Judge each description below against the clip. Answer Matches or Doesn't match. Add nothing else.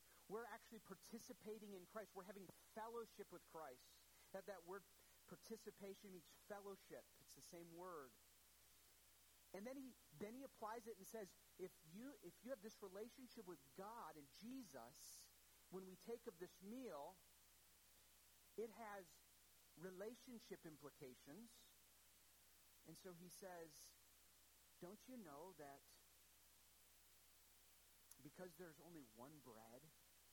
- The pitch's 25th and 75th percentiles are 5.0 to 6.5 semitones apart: Matches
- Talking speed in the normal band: Doesn't match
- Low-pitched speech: Doesn't match